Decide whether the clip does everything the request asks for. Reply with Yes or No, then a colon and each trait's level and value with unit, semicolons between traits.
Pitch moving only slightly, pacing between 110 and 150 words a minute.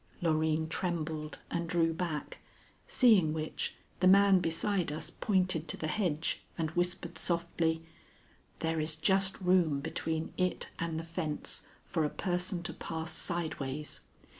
Yes: narrow, 2.2 semitones; average, 140 wpm